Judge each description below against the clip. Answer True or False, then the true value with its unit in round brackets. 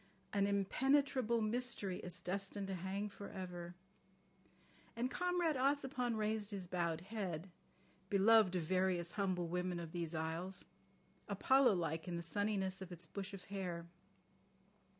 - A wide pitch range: False (3.7 semitones)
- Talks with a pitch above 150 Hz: True (190 Hz)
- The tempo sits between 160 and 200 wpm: False (140 wpm)